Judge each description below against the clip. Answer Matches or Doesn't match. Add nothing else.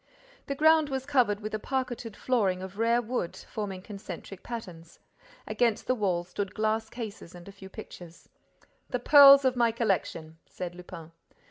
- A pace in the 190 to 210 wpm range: Doesn't match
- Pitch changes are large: Doesn't match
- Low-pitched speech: Doesn't match